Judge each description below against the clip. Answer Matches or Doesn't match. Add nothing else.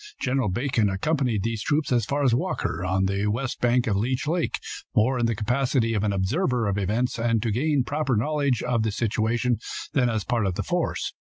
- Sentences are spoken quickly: Matches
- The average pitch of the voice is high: Doesn't match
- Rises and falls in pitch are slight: Doesn't match